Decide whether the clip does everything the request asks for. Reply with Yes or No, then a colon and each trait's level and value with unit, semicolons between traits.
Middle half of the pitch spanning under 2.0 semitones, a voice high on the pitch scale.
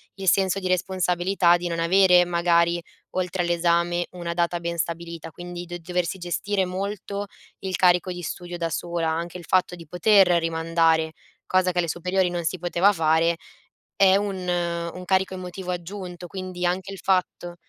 No: narrow, 1.5 semitones; medium, 175 Hz